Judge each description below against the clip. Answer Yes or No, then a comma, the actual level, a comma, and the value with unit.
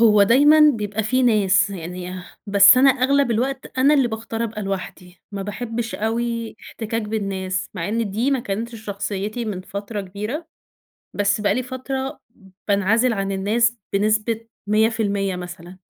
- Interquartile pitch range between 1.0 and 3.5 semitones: Yes, average, 3.0 semitones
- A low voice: No, high, 215 Hz